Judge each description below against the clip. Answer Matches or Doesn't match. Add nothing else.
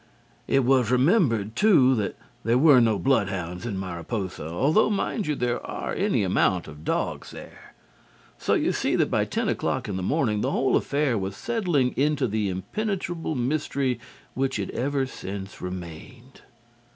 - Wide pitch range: Matches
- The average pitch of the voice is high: Doesn't match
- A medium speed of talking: Matches